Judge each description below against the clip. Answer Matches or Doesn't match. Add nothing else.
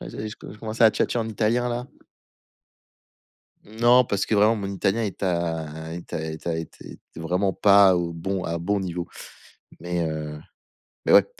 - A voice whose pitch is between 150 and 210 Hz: Doesn't match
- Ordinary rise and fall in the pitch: Matches